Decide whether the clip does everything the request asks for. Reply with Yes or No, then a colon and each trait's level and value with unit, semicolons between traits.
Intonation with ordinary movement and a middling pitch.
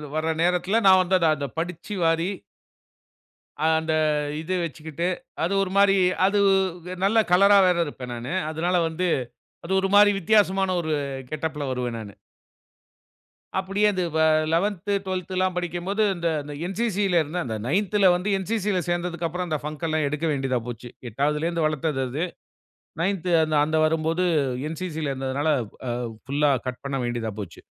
Yes: average, 3.8 semitones; medium, 170 Hz